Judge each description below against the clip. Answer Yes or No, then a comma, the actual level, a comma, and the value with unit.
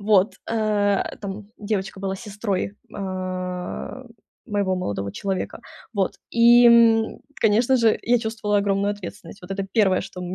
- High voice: Yes, high, 205 Hz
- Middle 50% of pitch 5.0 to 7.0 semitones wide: No, narrow, 2.6 semitones